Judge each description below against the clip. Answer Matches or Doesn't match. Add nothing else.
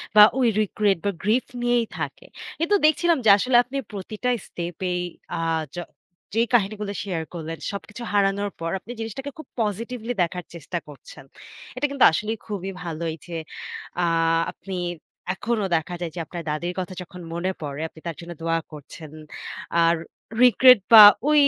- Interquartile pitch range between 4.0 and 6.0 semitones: Matches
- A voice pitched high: Matches